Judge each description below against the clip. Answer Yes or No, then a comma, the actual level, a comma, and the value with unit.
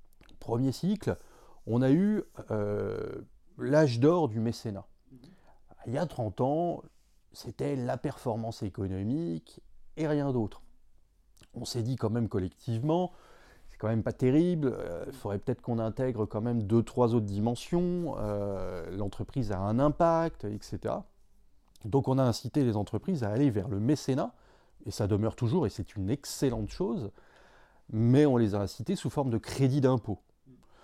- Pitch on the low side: Yes, low, 120 Hz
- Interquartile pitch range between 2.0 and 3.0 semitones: No, average, 5.0 semitones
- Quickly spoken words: No, average, 160 wpm